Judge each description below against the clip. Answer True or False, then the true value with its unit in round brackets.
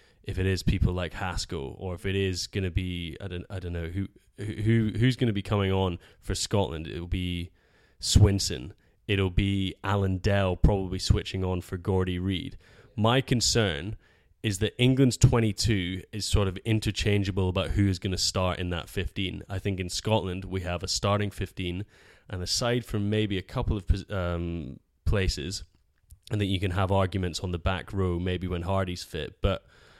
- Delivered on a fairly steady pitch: True (2.3 semitones)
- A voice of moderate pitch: False (95 Hz)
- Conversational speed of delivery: True (180 wpm)